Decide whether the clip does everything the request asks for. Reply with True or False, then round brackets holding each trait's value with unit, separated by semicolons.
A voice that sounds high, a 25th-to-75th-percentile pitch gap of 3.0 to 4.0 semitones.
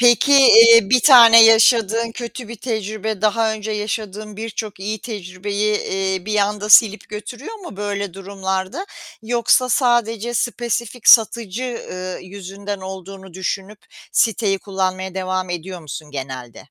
True (210 Hz; 3.3 semitones)